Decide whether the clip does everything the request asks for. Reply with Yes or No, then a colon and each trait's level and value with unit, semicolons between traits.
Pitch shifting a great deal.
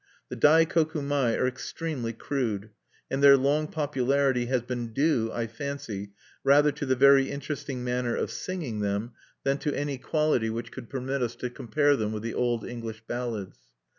No: average, 3.4 semitones